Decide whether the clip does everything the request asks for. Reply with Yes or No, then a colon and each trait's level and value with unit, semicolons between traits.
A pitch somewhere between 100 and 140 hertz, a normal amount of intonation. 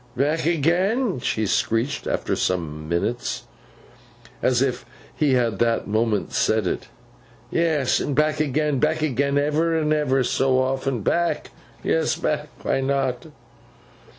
Yes: low, 135 Hz; average, 4.5 semitones